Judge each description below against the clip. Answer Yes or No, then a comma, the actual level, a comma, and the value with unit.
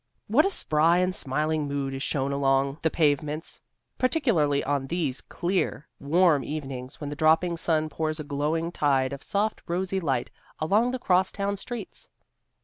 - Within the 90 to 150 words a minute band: No, average, 160 wpm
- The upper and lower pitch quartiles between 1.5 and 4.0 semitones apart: No, average, 4.4 semitones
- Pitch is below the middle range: No, medium, 155 Hz